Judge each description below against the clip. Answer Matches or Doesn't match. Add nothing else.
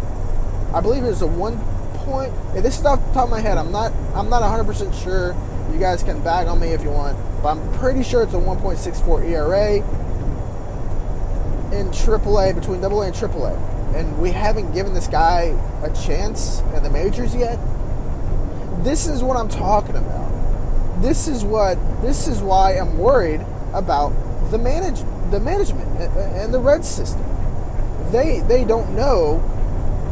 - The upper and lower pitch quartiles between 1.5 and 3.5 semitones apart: Doesn't match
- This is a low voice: Matches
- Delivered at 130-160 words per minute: Doesn't match